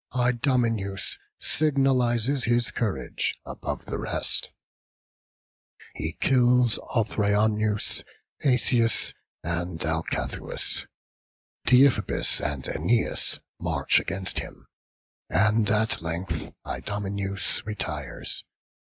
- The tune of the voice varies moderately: Yes, average, 3.9 semitones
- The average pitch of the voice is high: No, low, 110 Hz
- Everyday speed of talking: No, slow, 75 wpm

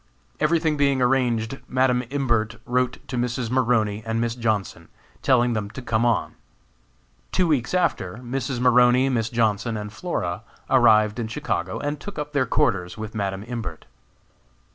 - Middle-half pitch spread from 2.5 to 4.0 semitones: Yes, average, 3.2 semitones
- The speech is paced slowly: No, average, 150 wpm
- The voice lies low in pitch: Yes, low, 120 Hz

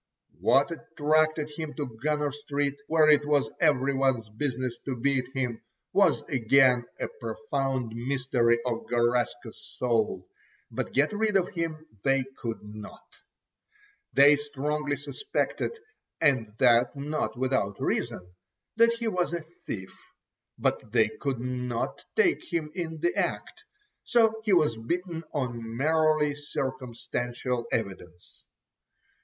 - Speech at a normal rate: No, slow, 125 wpm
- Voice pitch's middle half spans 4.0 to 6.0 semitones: Yes, average, 4.4 semitones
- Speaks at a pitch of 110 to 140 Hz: Yes, low, 135 Hz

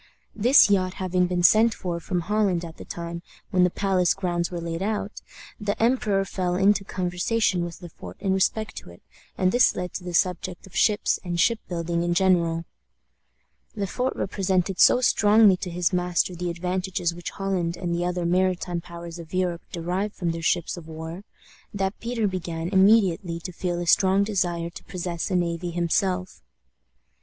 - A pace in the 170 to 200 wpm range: Yes, average, 180 wpm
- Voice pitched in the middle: Yes, medium, 180 Hz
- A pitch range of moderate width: No, narrow, 2.2 semitones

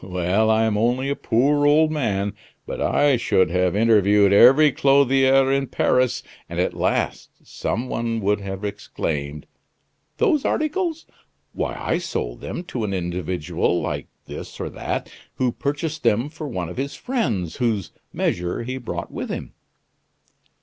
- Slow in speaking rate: No, average, 150 wpm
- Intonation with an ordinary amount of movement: No, wide, 6.5 semitones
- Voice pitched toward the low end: Yes, low, 115 Hz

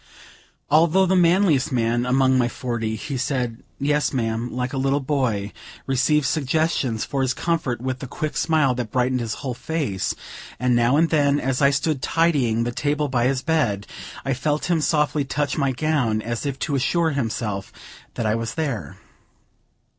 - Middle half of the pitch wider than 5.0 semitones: No, average, 3.8 semitones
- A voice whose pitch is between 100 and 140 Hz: Yes, low, 135 Hz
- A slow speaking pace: No, average, 175 wpm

